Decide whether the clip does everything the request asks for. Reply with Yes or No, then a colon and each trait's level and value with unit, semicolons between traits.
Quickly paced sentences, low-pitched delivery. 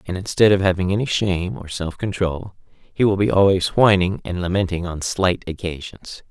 No: average, 180 wpm; very low, 95 Hz